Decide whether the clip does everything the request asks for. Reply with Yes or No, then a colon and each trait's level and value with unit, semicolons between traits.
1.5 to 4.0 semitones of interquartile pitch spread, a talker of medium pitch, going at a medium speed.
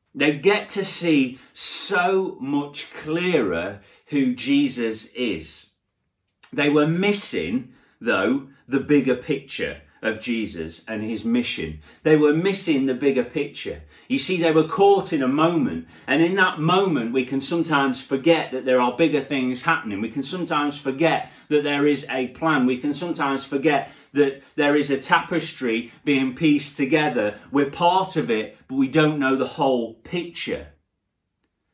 No: average, 4.5 semitones; medium, 145 Hz; average, 155 wpm